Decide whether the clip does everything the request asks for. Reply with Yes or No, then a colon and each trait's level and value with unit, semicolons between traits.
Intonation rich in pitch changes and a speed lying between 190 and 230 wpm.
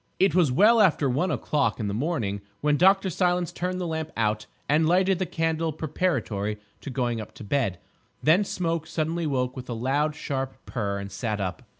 Yes: wide, 6.4 semitones; average, 195 wpm